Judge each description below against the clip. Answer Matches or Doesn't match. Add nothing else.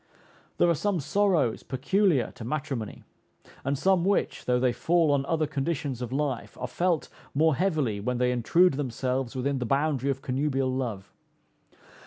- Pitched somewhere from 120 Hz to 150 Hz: Matches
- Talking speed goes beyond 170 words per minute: Doesn't match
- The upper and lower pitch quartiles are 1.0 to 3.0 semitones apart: Doesn't match